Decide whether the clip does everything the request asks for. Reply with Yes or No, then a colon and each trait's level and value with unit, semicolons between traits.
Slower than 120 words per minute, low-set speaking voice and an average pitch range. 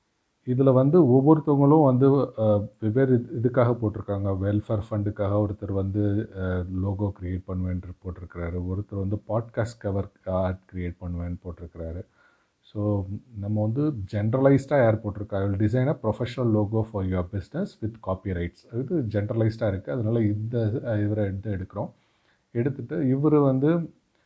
No: average, 125 wpm; low, 105 Hz; average, 4.3 semitones